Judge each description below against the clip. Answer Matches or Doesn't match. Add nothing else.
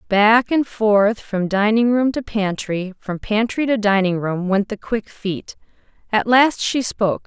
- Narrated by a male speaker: Doesn't match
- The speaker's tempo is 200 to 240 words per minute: Doesn't match